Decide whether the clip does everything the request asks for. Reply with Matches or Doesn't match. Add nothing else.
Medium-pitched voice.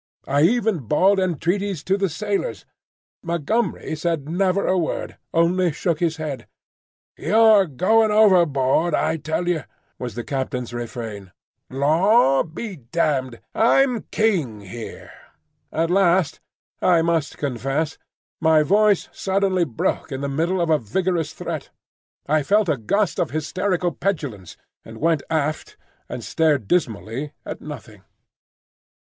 Matches